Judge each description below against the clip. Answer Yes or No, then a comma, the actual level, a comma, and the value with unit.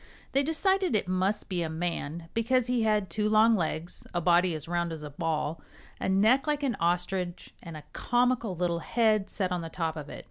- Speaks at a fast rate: Yes, fast, 210 wpm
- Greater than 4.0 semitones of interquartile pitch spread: Yes, average, 5.2 semitones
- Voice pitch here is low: No, medium, 185 Hz